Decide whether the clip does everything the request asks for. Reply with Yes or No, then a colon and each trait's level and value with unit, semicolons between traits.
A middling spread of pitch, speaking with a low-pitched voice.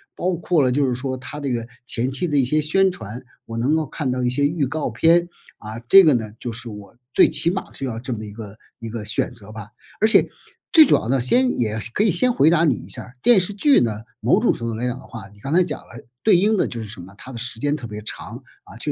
No: wide, 6.4 semitones; low, 130 Hz